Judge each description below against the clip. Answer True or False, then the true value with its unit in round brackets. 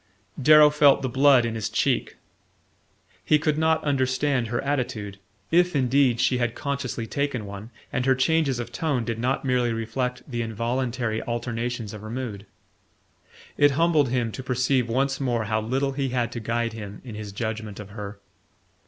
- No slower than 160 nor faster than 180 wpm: True (170 wpm)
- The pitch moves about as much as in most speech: True (3.3 semitones)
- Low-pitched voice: True (125 Hz)